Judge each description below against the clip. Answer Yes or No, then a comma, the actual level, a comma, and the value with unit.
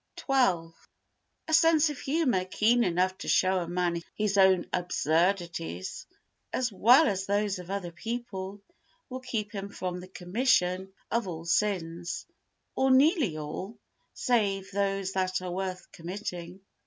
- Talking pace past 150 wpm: No, average, 140 wpm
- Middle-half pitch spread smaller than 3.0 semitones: No, average, 4.1 semitones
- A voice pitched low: No, high, 190 Hz